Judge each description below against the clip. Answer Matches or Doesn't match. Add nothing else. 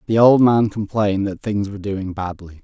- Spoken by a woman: Doesn't match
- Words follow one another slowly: Doesn't match